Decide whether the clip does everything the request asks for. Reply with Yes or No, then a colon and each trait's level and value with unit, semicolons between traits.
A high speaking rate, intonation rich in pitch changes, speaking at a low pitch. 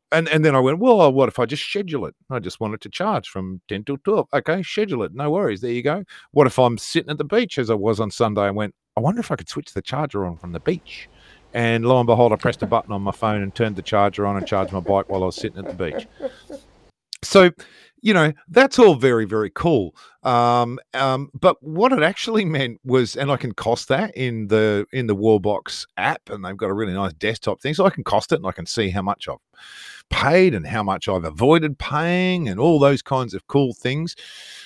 Yes: fast, 250 wpm; wide, 6.8 semitones; low, 130 Hz